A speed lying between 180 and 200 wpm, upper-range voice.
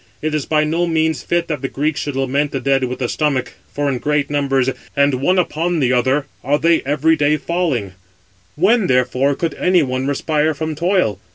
No: average, 195 wpm; medium, 145 Hz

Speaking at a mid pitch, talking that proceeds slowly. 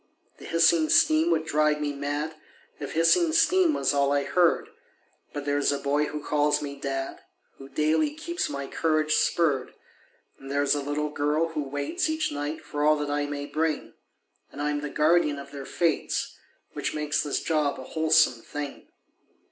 No: medium, 150 Hz; average, 175 wpm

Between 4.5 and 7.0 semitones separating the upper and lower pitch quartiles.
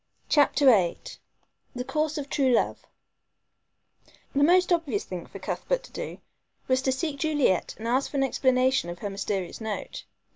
Yes: average, 5.2 semitones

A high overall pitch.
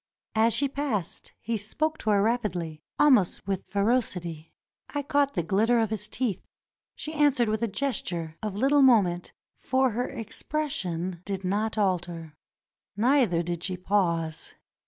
Yes: high, 210 Hz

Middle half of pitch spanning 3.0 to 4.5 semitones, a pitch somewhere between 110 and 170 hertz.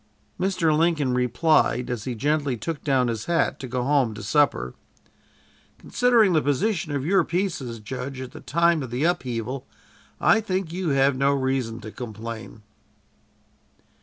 No: average, 5.2 semitones; medium, 140 Hz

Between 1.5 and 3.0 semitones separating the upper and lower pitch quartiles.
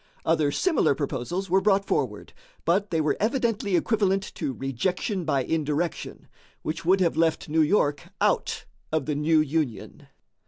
No: average, 4.4 semitones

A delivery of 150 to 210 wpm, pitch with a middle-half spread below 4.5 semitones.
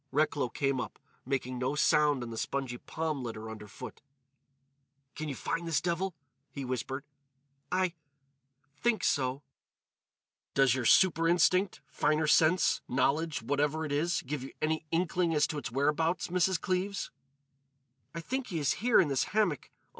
No: slow, 135 wpm; average, 3.9 semitones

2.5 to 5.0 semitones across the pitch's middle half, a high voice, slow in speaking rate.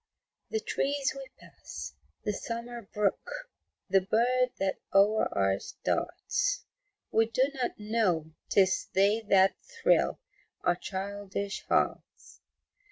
Yes: average, 4.5 semitones; high, 210 Hz; slow, 110 wpm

